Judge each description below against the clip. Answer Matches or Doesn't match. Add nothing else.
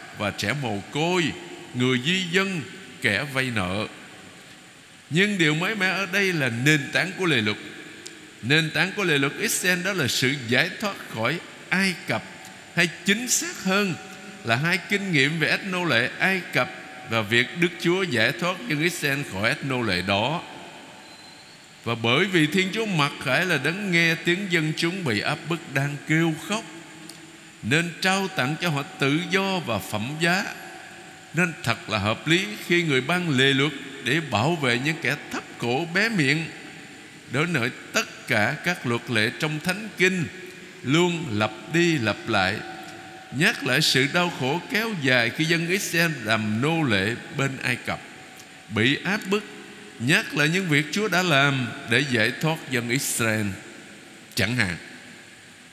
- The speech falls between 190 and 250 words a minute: Doesn't match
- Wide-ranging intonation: Matches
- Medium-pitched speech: Matches